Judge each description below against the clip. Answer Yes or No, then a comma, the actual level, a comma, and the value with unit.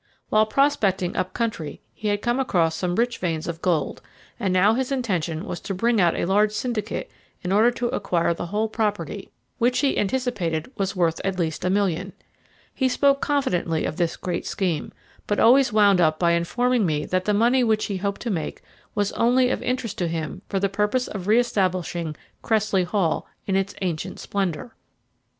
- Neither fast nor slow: Yes, average, 190 wpm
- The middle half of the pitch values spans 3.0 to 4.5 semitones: No, average, 4.9 semitones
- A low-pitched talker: No, high, 200 Hz